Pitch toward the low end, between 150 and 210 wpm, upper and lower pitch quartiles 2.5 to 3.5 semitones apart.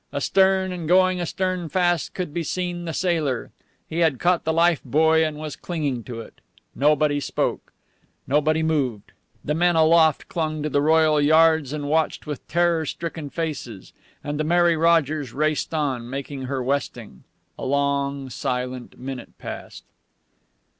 No: medium, 155 Hz; average, 155 wpm; average, 3.1 semitones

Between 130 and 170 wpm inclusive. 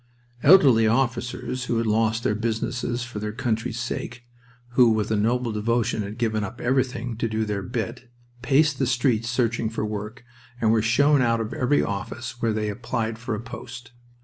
No: average, 180 wpm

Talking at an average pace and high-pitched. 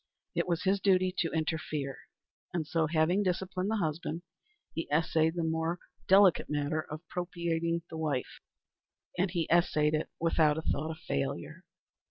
No: average, 155 wpm; medium, 165 Hz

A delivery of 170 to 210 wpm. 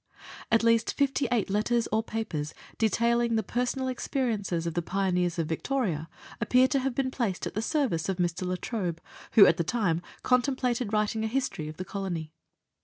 Yes: average, 180 wpm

